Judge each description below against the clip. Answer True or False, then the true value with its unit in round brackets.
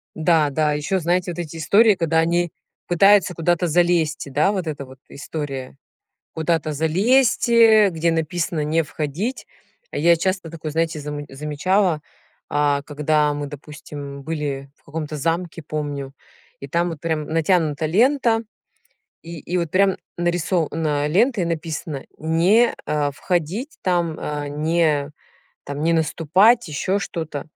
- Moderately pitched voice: True (160 Hz)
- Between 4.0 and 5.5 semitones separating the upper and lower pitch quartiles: False (3.0 semitones)